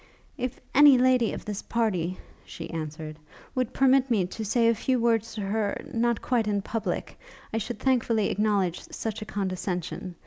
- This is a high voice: Yes, high, 220 Hz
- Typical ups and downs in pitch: Yes, average, 3.8 semitones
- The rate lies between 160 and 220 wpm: Yes, average, 170 wpm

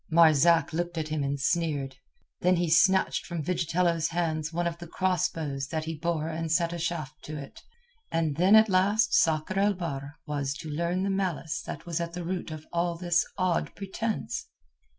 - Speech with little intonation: Yes, narrow, 2.2 semitones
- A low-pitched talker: No, medium, 170 Hz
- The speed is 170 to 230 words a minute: Yes, average, 190 wpm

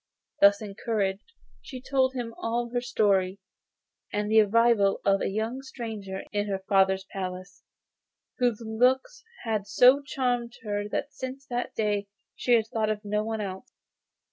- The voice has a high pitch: Yes, high, 220 Hz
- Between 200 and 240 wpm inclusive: No, average, 155 wpm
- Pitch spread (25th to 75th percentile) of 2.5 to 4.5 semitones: Yes, average, 3.4 semitones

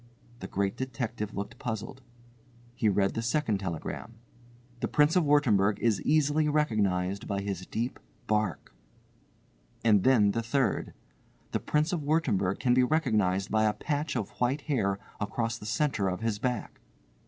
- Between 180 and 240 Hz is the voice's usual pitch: No, low, 115 Hz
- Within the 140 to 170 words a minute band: Yes, average, 155 wpm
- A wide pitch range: Yes, wide, 5.7 semitones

